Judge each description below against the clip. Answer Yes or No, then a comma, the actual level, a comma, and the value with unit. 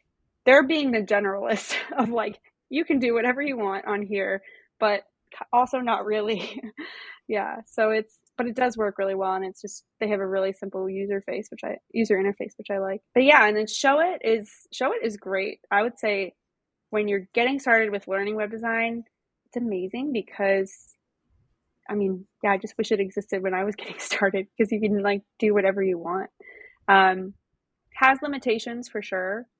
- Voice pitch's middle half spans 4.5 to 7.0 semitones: No, average, 3.2 semitones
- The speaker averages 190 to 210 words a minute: Yes, average, 195 wpm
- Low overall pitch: No, high, 215 Hz